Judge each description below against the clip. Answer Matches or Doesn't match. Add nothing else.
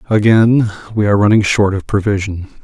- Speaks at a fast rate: Doesn't match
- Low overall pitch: Matches